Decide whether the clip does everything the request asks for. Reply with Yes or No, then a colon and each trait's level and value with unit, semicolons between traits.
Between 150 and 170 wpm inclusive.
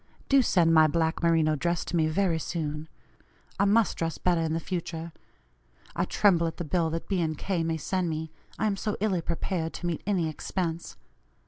No: average, 200 wpm